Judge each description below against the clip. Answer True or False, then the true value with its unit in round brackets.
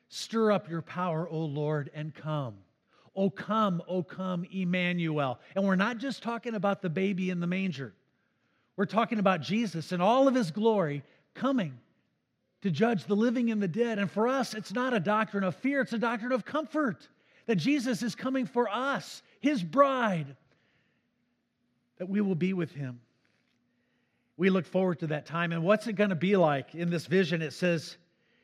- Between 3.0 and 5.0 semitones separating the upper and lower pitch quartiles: False (5.5 semitones)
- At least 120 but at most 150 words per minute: False (185 wpm)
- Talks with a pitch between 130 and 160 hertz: False (190 Hz)